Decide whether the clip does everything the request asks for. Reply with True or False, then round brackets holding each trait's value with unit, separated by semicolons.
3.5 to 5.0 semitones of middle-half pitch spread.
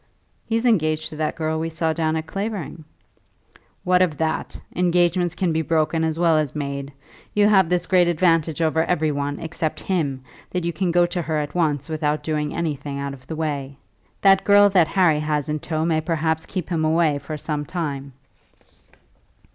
False (2.5 semitones)